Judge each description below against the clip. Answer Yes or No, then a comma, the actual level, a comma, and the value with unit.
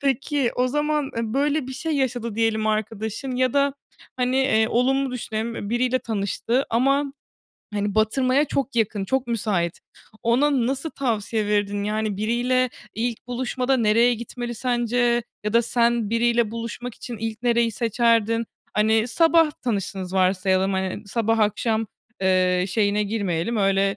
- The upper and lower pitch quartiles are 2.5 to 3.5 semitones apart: Yes, average, 3.2 semitones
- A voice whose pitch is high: Yes, high, 230 Hz